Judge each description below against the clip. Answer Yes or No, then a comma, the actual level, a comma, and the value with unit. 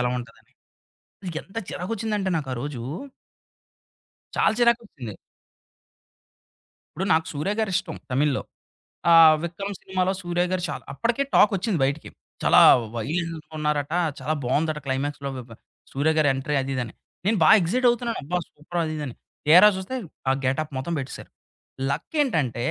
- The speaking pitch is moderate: Yes, medium, 160 Hz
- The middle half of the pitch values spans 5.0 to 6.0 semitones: Yes, average, 5.3 semitones